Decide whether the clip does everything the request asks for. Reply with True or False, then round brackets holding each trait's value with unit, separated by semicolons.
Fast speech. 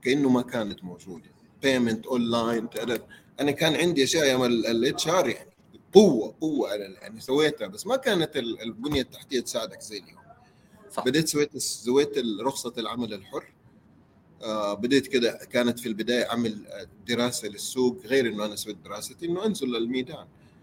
True (140 wpm)